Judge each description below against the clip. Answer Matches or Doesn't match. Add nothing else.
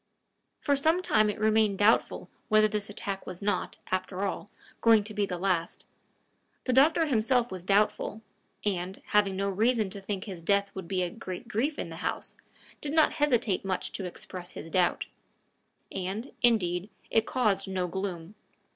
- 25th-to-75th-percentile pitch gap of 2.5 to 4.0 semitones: Matches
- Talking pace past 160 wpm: Matches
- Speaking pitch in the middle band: Doesn't match